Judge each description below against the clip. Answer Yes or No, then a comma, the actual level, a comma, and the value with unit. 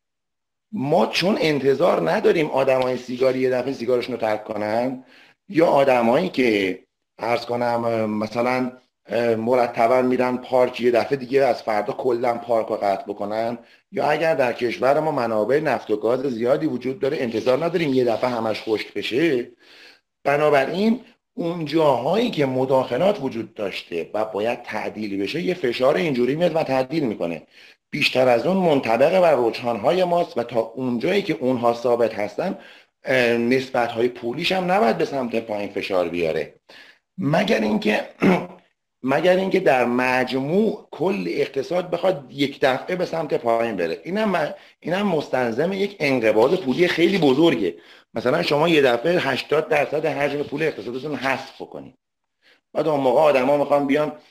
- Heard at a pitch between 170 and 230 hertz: No, low, 130 Hz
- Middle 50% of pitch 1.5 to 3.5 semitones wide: No, average, 4.3 semitones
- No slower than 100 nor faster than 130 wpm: No, average, 150 wpm